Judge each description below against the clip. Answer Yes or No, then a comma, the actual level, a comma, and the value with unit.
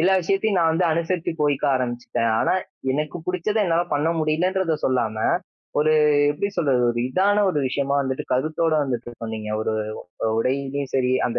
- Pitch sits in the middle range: Yes, medium, 150 Hz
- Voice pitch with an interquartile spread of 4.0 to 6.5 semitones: Yes, average, 5.1 semitones